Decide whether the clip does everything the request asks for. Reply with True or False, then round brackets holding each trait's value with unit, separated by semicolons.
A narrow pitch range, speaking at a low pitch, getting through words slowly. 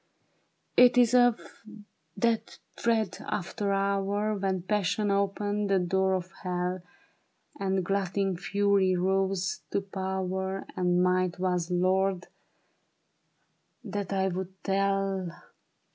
False (1.4 semitones; 190 Hz; 105 wpm)